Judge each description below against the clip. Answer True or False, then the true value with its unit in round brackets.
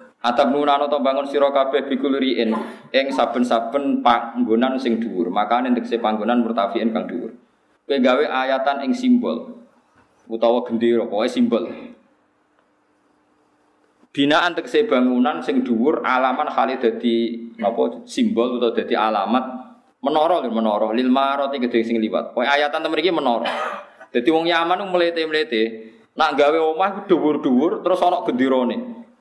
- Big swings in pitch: True (6.0 semitones)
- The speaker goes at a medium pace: True (130 wpm)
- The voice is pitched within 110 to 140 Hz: True (135 Hz)